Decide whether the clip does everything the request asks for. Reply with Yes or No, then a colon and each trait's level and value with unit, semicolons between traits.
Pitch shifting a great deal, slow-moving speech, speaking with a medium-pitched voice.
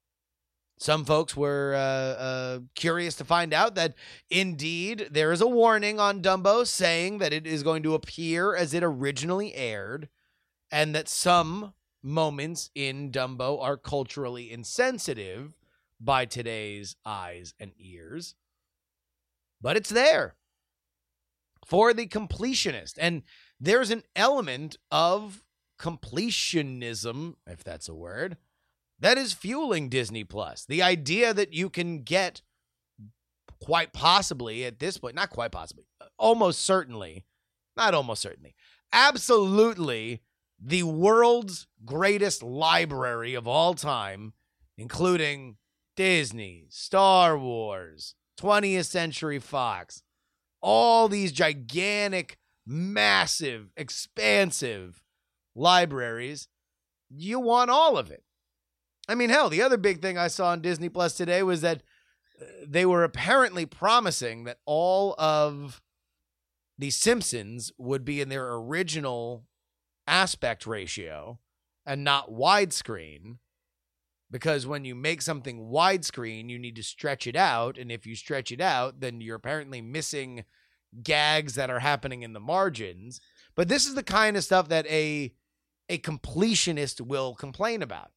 Yes: wide, 7.4 semitones; slow, 125 wpm; medium, 150 Hz